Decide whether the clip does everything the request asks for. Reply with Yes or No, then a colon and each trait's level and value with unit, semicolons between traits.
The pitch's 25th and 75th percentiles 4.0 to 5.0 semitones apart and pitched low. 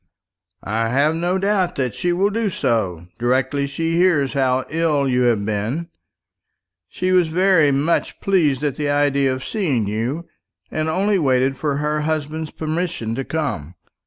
No: average, 4.5 semitones; medium, 145 Hz